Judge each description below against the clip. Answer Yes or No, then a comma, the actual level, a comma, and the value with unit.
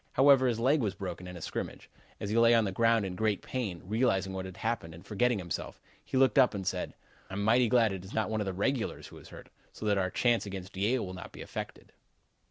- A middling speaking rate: No, fast, 250 wpm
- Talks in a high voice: No, low, 105 Hz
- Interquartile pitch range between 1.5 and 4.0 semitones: Yes, average, 3.7 semitones